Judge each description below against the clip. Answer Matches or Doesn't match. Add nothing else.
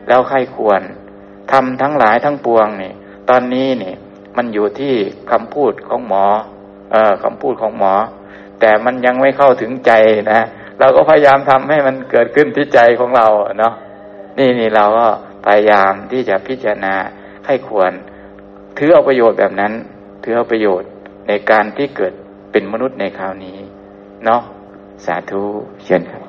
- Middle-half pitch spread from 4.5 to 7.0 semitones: Doesn't match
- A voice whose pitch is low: Matches